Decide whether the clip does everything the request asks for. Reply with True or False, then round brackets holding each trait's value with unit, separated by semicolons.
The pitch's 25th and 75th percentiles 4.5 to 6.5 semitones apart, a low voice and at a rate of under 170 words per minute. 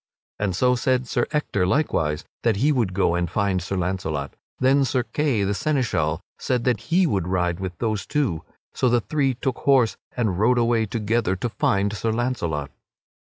False (5.5 semitones; 110 Hz; 180 wpm)